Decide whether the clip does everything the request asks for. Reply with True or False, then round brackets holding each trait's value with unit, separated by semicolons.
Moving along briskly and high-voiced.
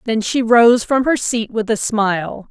True (215 wpm; 225 Hz)